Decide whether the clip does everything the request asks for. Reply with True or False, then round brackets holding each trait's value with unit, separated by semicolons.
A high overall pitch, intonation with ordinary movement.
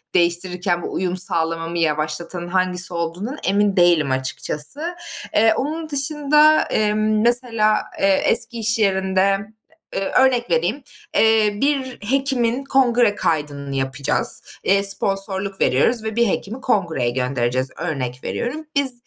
False (195 Hz; 6.1 semitones)